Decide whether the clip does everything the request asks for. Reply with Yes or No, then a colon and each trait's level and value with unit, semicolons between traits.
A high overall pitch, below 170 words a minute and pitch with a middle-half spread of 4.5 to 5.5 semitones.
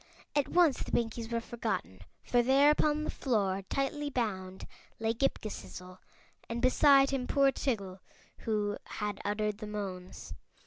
Yes: high, 225 Hz; average, 145 wpm; average, 5.0 semitones